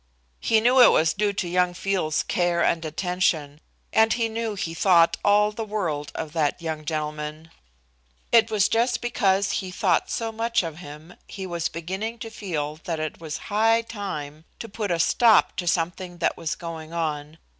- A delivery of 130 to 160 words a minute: No, average, 180 wpm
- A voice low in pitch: No, medium, 180 Hz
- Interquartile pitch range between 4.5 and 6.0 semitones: Yes, average, 4.9 semitones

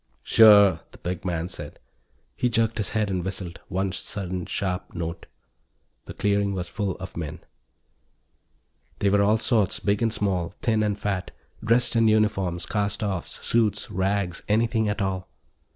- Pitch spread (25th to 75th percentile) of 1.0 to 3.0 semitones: Yes, average, 2.7 semitones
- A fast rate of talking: No, average, 155 wpm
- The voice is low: Yes, low, 100 Hz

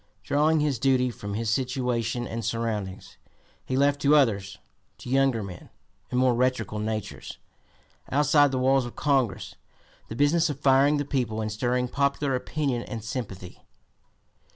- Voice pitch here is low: Yes, low, 125 Hz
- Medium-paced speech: Yes, average, 150 wpm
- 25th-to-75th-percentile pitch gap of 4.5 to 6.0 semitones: No, average, 3.7 semitones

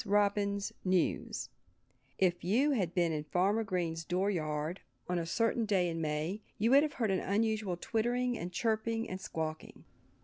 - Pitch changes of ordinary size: Yes, average, 4.2 semitones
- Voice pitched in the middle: No, high, 195 Hz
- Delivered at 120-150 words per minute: No, average, 165 wpm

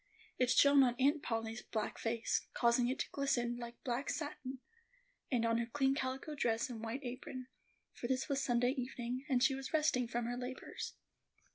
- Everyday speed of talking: Yes, average, 180 wpm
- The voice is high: Yes, very high, 250 Hz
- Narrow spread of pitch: Yes, narrow, 2.2 semitones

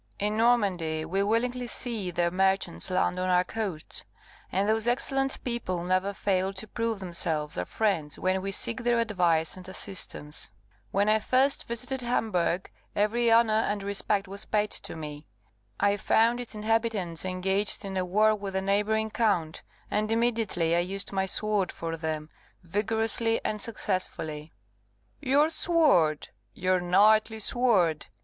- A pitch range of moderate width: Yes, average, 3.7 semitones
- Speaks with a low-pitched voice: No, high, 200 Hz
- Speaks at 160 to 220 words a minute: No, average, 150 wpm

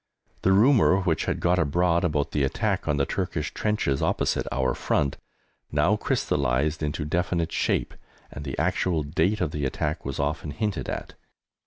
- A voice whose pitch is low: Yes, very low, 80 Hz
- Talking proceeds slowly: No, average, 165 wpm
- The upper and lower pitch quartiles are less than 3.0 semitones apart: No, average, 3.8 semitones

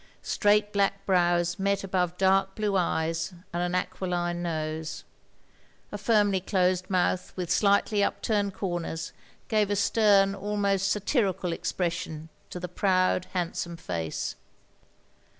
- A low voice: No, medium, 185 Hz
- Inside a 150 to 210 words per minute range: No, slow, 135 wpm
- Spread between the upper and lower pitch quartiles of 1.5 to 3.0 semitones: Yes, narrow, 2.4 semitones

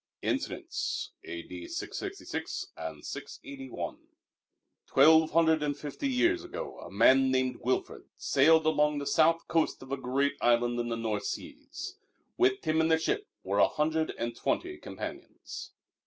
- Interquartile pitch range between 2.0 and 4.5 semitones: Yes, average, 4.0 semitones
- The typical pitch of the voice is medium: Yes, medium, 145 Hz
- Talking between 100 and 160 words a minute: Yes, average, 145 wpm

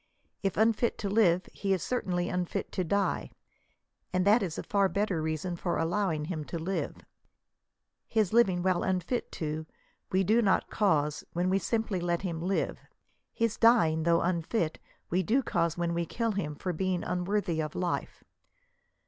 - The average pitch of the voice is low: No, medium, 185 Hz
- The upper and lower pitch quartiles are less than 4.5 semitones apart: Yes, average, 3.1 semitones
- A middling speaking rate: Yes, average, 170 wpm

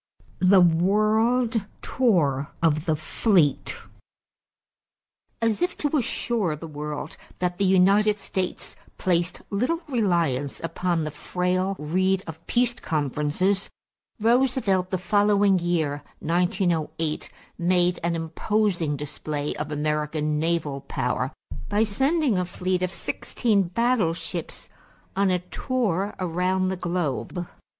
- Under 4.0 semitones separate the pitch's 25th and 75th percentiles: No, average, 4.4 semitones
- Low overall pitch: No, medium, 180 Hz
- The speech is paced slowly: Yes, slow, 115 wpm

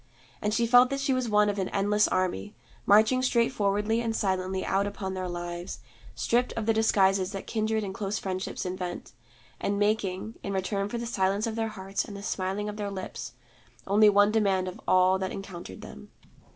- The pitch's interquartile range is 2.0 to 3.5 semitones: Yes, narrow, 2.5 semitones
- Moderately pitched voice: No, high, 200 Hz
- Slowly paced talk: No, average, 190 wpm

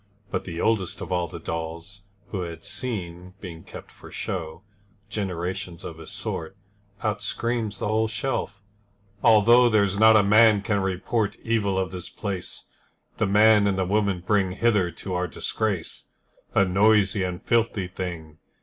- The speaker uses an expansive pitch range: No, average, 3.2 semitones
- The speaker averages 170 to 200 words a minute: No, average, 160 wpm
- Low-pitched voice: Yes, low, 100 Hz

